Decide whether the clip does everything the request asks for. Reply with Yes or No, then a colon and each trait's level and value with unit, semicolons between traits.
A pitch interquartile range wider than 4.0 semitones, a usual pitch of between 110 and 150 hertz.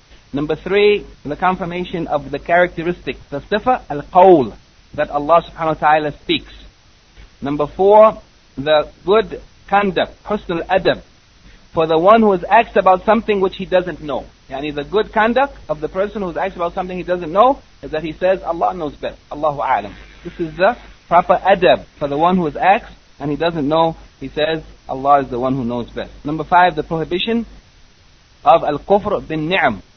No: average, 4.6 semitones; medium, 170 Hz